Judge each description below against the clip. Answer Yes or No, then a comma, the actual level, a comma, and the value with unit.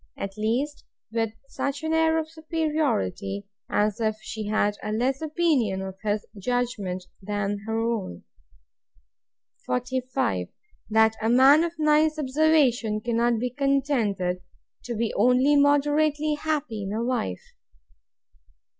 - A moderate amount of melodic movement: No, wide, 5.7 semitones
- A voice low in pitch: No, high, 245 Hz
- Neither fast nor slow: No, slow, 125 wpm